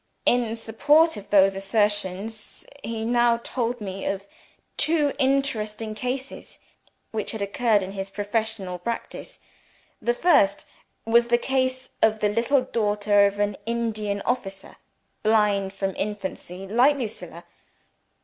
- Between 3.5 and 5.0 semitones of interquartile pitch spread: No, average, 3.0 semitones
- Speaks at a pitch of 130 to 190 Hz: No, high, 220 Hz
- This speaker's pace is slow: Yes, slow, 125 wpm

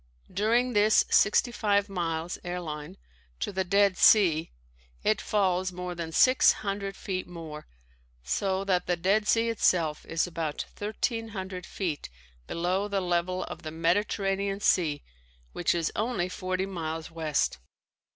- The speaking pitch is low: No, medium, 185 Hz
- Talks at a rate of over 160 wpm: No, average, 140 wpm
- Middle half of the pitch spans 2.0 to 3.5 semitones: Yes, average, 3.2 semitones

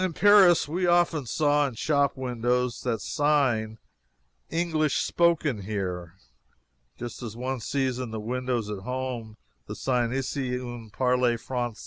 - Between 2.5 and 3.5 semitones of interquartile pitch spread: No, average, 4.0 semitones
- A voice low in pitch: Yes, low, 125 Hz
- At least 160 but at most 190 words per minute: No, average, 140 wpm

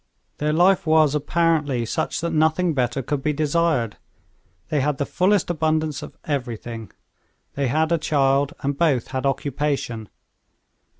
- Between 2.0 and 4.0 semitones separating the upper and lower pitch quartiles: Yes, average, 2.9 semitones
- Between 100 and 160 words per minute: Yes, average, 140 wpm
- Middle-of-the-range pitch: Yes, medium, 150 Hz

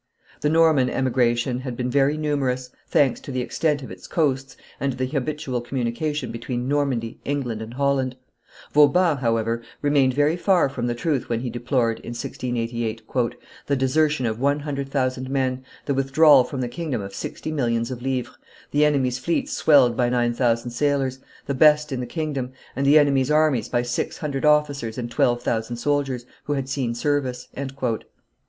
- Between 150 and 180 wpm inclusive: Yes, average, 175 wpm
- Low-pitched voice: Yes, low, 130 Hz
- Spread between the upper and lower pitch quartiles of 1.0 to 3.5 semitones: Yes, average, 3.0 semitones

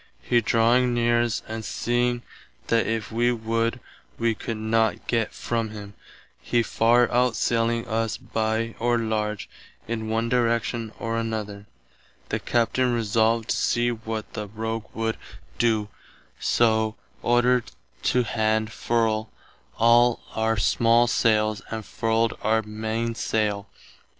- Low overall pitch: Yes, low, 115 Hz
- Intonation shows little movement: Yes, narrow, 1.2 semitones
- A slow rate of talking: Yes, slow, 125 wpm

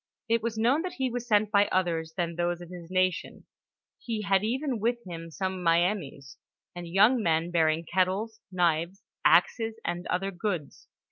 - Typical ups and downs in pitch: Yes, average, 4.3 semitones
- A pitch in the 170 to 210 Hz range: Yes, medium, 185 Hz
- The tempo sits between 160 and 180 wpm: Yes, average, 165 wpm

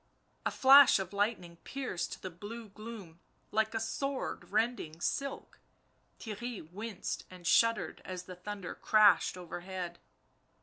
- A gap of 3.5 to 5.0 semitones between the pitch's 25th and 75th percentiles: Yes, average, 4.1 semitones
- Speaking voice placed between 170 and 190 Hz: No, high, 205 Hz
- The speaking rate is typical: No, slow, 125 wpm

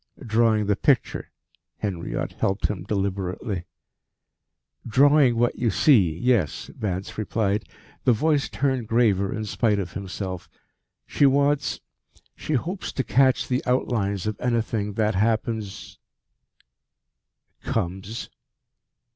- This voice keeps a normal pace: No, slow, 115 wpm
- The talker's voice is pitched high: No, low, 110 Hz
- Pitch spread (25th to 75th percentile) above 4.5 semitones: No, average, 4.2 semitones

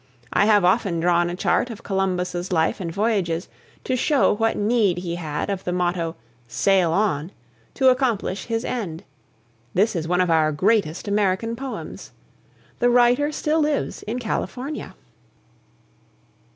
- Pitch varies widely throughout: No, average, 4.9 semitones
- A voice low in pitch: No, high, 195 Hz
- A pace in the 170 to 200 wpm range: No, average, 145 wpm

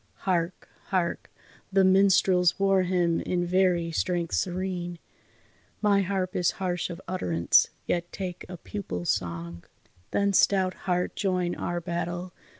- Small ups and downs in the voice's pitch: Yes, narrow, 1.6 semitones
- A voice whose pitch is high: No, medium, 180 Hz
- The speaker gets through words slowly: Yes, slow, 130 wpm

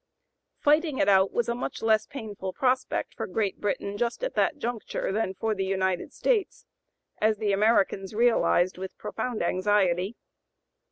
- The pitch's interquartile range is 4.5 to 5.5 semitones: No, average, 3.8 semitones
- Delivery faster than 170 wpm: No, average, 155 wpm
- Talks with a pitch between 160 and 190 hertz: No, high, 215 Hz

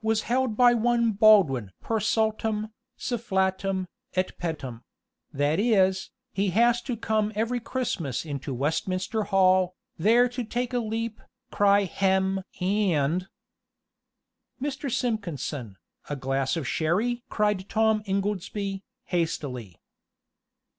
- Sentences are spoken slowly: Yes, slow, 115 wpm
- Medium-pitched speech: No, high, 200 Hz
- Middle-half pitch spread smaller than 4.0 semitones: No, average, 4.4 semitones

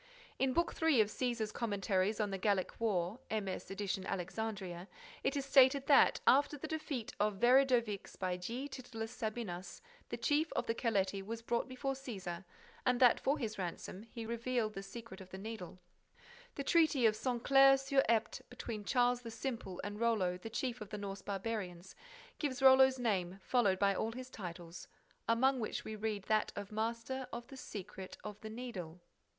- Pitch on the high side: Yes, high, 225 Hz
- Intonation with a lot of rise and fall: No, average, 4.5 semitones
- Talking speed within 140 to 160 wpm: No, average, 180 wpm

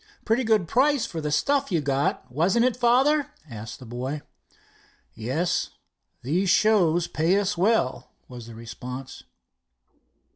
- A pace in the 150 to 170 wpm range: No, slow, 135 wpm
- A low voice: No, medium, 170 Hz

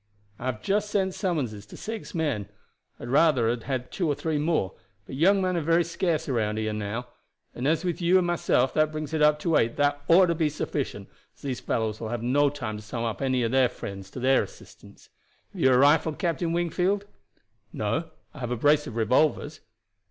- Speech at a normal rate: No, fast, 215 wpm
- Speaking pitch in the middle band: Yes, medium, 145 Hz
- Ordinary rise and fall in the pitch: No, wide, 5.8 semitones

